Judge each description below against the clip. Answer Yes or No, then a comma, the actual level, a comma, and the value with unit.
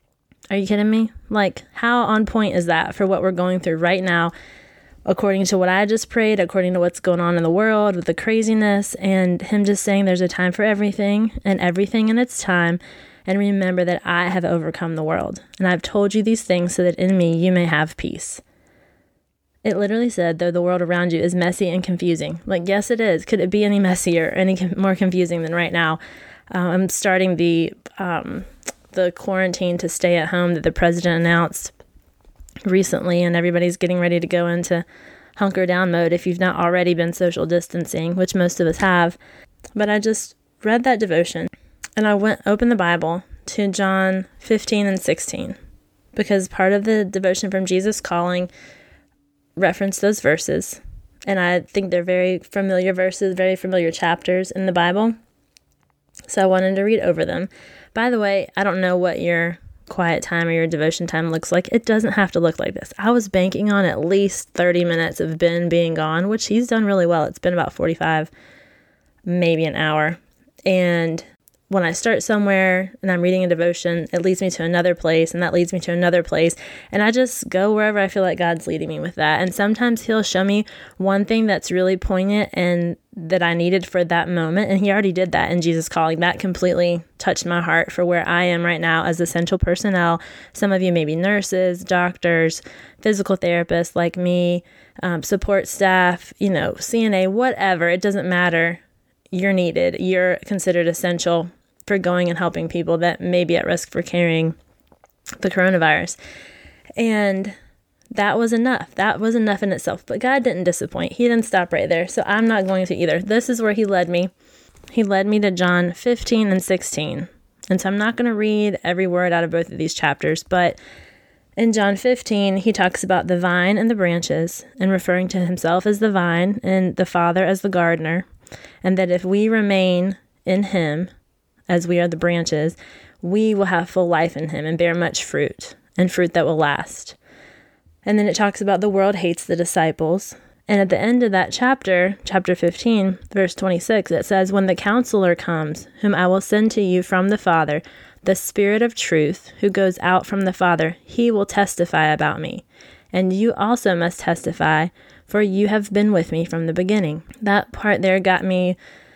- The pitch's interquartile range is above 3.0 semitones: No, average, 2.7 semitones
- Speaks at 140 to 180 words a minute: No, average, 195 wpm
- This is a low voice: No, medium, 185 Hz